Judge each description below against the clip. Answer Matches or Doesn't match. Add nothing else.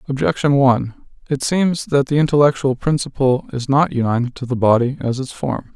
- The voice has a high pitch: Doesn't match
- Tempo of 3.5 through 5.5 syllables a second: Matches